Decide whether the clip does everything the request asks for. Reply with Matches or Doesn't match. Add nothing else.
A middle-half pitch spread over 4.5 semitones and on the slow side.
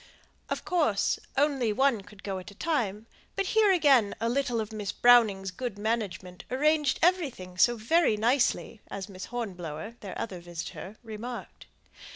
Doesn't match